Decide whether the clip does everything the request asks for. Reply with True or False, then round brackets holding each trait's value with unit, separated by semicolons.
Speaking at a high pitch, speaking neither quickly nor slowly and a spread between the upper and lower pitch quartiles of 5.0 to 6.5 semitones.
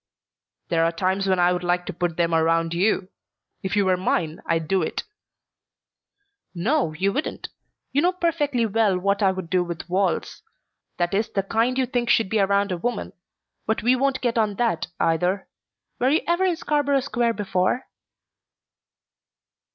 True (195 Hz; 175 wpm; 5.4 semitones)